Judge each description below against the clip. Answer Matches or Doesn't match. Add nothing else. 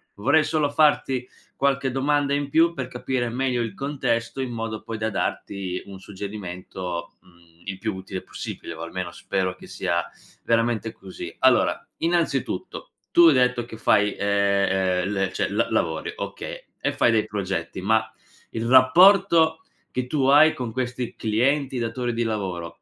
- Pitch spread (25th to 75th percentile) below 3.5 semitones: Doesn't match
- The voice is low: Matches